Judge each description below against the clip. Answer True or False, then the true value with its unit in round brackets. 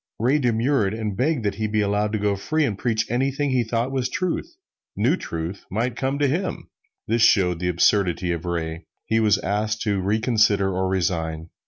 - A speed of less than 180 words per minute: False (190 wpm)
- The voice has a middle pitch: False (110 Hz)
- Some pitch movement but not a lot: True (4.7 semitones)